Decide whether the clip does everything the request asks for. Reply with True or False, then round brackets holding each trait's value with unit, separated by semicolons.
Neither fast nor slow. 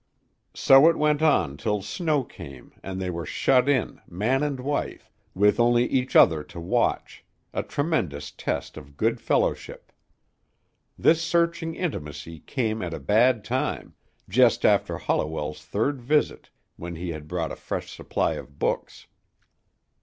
True (145 wpm)